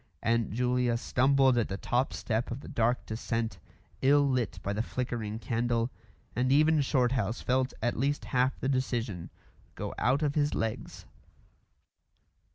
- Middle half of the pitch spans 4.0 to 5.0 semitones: No, narrow, 2.6 semitones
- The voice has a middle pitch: No, low, 125 Hz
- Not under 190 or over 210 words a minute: No, average, 150 wpm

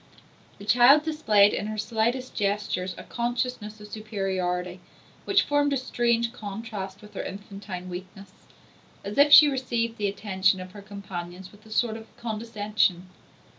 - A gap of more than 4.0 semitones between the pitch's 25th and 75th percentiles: No, average, 3.3 semitones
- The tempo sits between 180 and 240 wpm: No, average, 150 wpm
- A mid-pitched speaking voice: No, high, 210 Hz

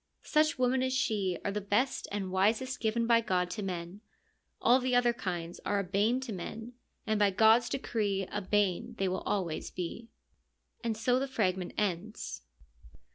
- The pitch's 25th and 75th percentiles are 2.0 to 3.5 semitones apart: No, average, 4.1 semitones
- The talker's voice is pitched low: No, high, 210 Hz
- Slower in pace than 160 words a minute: No, average, 180 wpm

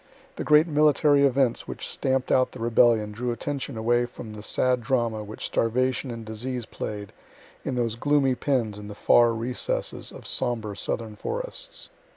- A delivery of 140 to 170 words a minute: Yes, average, 165 wpm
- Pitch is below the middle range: Yes, low, 120 Hz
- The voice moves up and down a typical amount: Yes, average, 3.0 semitones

